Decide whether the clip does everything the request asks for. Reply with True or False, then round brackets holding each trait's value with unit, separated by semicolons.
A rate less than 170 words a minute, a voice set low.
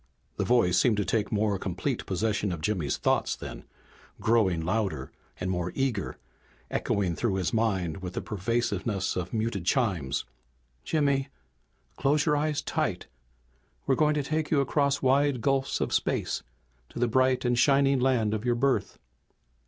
True (155 wpm; 115 Hz)